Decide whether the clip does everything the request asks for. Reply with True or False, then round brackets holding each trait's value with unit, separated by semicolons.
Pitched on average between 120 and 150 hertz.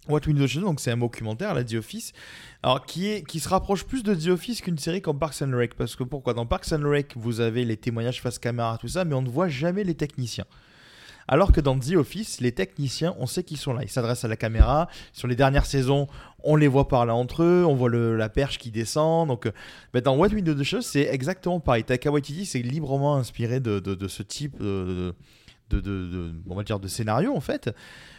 True (135 Hz)